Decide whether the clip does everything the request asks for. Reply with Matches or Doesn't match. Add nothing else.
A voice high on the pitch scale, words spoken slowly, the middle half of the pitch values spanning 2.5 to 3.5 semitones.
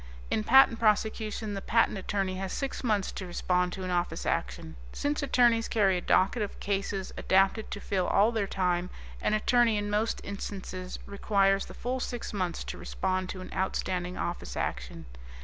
Doesn't match